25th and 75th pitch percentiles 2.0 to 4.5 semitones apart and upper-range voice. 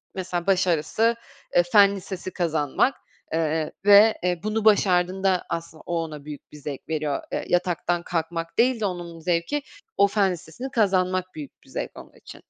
No: average, 3.3 semitones; medium, 180 Hz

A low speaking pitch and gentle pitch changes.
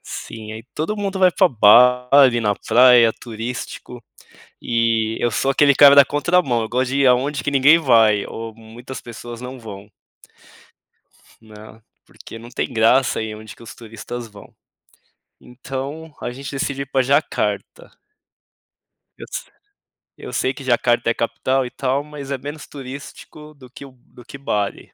No: low, 125 Hz; average, 3.5 semitones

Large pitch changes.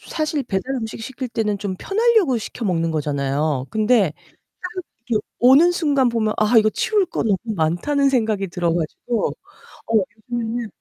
Yes: wide, 5.8 semitones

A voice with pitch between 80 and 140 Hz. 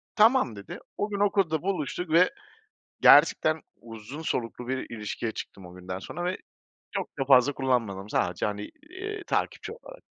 Yes: low, 135 Hz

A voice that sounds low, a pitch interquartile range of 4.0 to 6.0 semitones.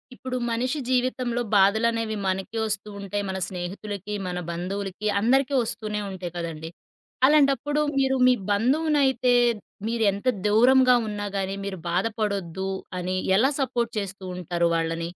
No: high, 210 Hz; average, 4.9 semitones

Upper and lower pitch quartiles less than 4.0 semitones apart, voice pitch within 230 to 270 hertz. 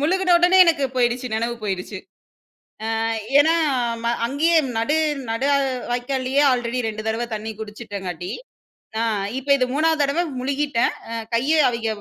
No: average, 4.6 semitones; very high, 255 Hz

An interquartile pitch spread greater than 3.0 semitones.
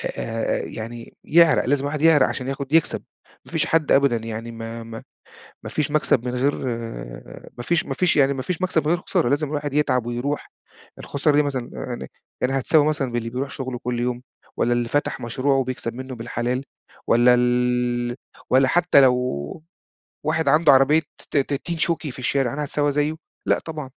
Yes: average, 3.5 semitones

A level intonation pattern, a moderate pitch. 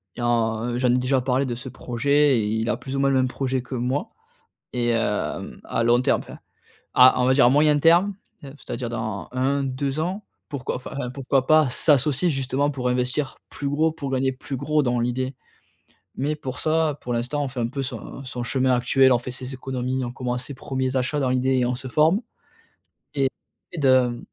No: narrow, 2.2 semitones; low, 130 Hz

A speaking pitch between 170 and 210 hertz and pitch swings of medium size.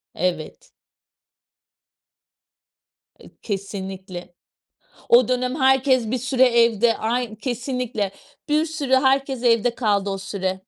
No: high, 235 Hz; average, 4.4 semitones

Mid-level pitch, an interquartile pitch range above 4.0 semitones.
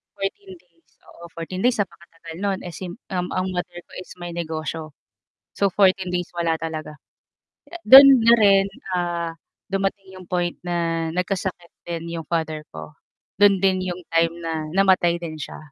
No: medium, 175 Hz; narrow, 2.4 semitones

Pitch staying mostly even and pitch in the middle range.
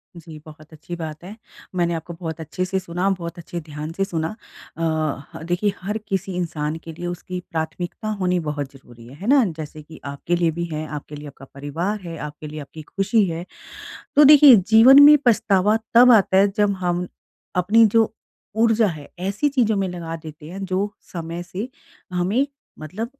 No: average, 4.2 semitones; medium, 175 Hz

